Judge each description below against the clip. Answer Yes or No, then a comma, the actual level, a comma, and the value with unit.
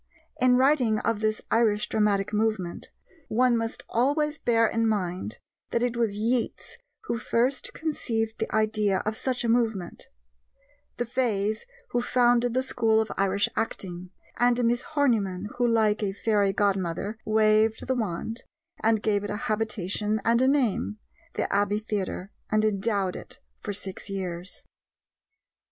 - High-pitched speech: Yes, high, 220 Hz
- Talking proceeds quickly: No, average, 145 wpm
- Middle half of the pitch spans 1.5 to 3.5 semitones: Yes, average, 2.8 semitones